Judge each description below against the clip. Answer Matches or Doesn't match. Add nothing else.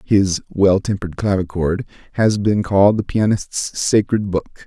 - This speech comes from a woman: Doesn't match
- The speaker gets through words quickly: Doesn't match